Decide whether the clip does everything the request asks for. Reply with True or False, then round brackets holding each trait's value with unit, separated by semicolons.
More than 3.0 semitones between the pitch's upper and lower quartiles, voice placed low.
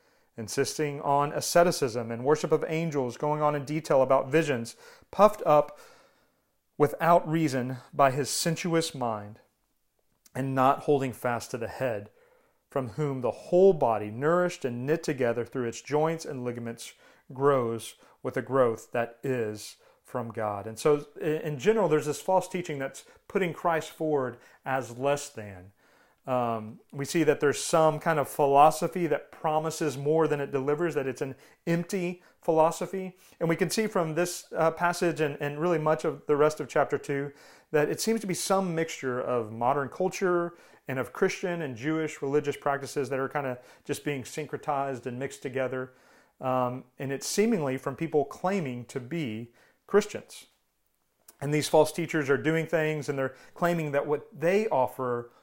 False (4.0 semitones; 150 Hz)